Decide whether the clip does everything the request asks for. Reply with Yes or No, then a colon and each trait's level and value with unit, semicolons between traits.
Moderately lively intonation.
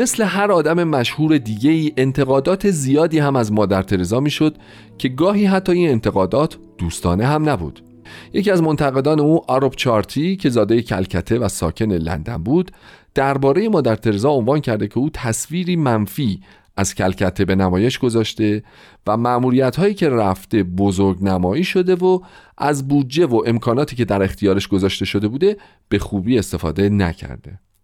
No: wide, 7.4 semitones